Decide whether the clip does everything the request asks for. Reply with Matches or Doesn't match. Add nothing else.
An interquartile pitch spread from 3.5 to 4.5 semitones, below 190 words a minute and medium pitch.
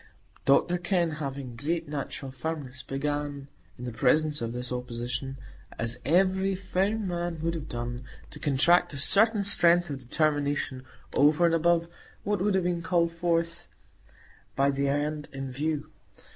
Matches